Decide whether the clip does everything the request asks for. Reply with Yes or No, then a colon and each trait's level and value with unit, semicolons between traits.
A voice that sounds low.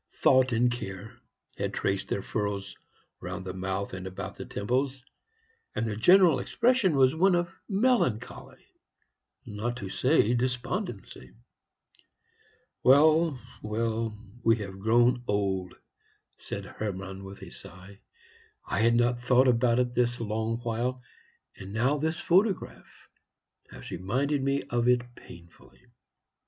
Yes: low, 120 Hz